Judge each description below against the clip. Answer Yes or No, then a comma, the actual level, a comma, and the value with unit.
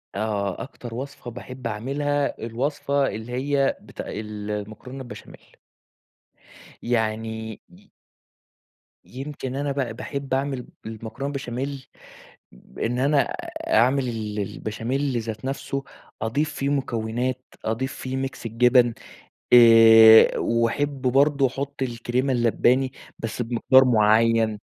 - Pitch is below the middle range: Yes, low, 125 Hz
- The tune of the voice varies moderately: Yes, average, 3.3 semitones